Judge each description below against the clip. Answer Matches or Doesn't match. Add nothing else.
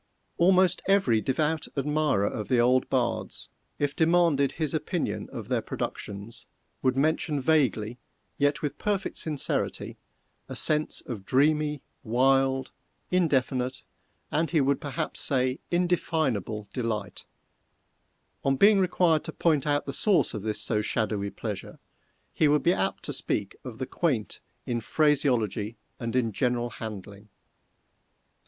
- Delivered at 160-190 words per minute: Doesn't match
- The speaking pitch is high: Doesn't match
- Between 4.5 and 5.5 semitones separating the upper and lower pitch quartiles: Matches